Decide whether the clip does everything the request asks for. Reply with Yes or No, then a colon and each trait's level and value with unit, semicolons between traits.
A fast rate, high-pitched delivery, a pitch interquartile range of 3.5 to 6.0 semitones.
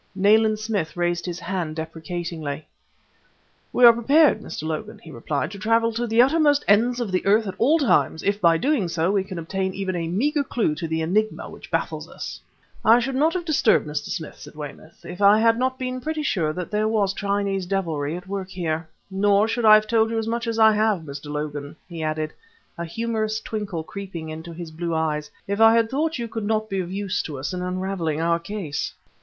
Yes: fast, 215 wpm; high, 195 Hz; average, 5.2 semitones